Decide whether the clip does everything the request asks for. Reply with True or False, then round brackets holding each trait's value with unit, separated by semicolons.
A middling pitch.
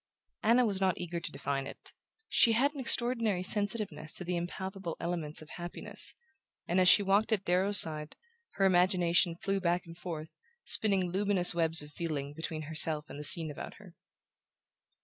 True (175 Hz)